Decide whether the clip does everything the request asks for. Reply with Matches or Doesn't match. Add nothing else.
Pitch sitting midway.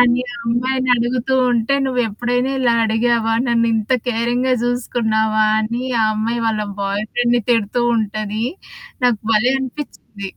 Doesn't match